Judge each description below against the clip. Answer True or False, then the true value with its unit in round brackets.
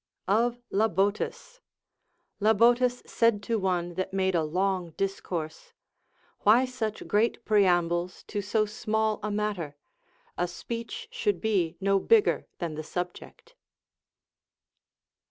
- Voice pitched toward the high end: True (205 Hz)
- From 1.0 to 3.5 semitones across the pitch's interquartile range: False (4.3 semitones)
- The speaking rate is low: True (115 wpm)